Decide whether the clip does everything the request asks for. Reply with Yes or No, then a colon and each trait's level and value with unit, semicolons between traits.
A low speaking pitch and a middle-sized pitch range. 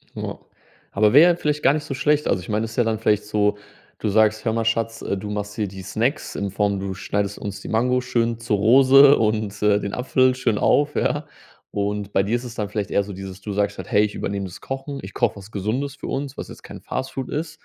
Yes: low, 110 Hz; average, 4.0 semitones